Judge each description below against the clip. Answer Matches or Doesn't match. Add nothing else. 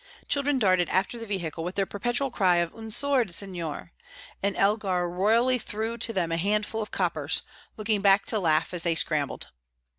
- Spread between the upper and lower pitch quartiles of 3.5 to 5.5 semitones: Matches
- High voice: Matches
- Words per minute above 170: Matches